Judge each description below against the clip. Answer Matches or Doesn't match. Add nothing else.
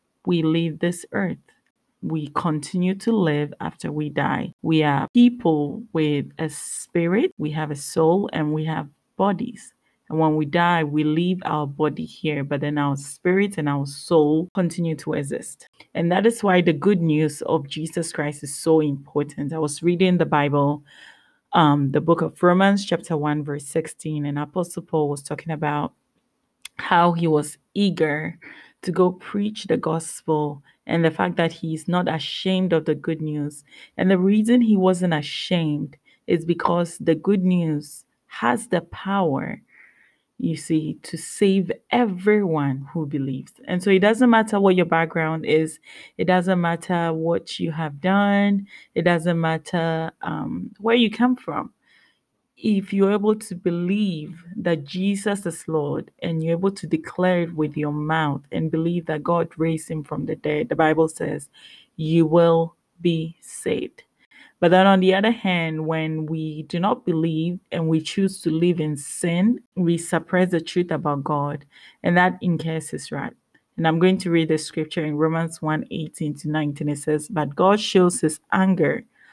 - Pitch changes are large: Doesn't match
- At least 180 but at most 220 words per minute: Doesn't match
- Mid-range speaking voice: Matches